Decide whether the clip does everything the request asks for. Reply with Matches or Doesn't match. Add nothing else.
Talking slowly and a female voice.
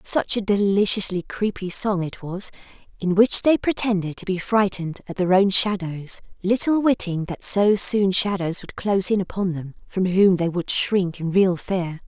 Doesn't match